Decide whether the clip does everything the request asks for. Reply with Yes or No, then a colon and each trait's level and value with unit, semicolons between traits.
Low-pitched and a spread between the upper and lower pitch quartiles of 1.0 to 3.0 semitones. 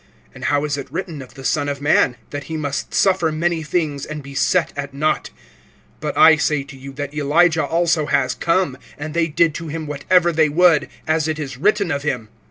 No: medium, 150 Hz; narrow, 2.6 semitones